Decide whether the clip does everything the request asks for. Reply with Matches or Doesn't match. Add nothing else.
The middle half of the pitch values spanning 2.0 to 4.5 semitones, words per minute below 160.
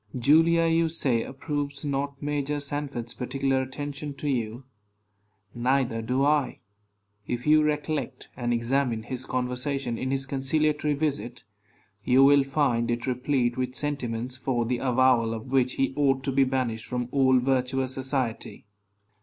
Matches